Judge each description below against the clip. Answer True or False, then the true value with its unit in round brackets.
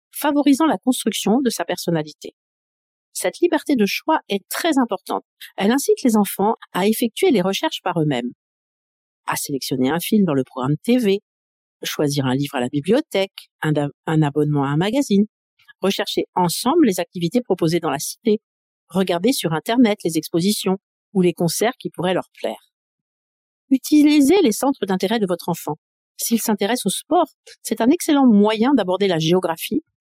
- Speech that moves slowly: False (165 wpm)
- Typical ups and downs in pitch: False (6.4 semitones)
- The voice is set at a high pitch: True (200 Hz)